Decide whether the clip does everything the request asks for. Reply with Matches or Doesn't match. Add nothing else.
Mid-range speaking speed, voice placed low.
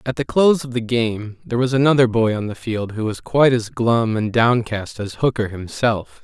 Doesn't match